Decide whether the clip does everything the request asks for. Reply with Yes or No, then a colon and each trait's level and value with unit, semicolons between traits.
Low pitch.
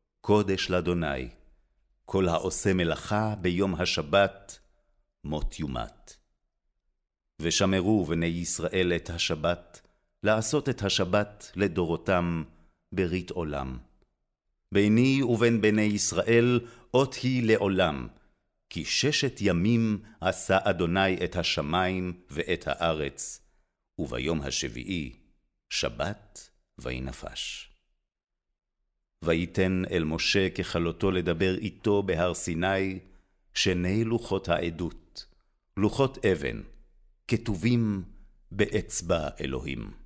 Yes: very low, 95 Hz